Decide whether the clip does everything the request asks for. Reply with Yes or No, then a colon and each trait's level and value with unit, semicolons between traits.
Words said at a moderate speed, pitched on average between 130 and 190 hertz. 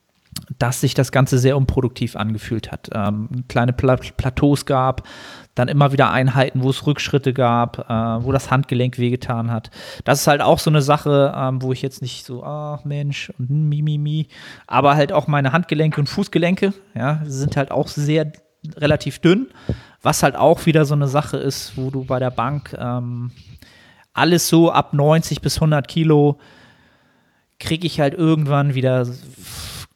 Yes: average, 170 wpm; medium, 140 Hz